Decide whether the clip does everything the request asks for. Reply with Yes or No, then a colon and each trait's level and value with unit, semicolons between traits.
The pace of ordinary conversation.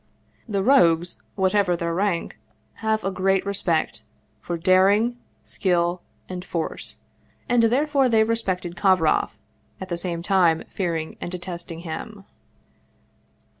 No: slow, 120 wpm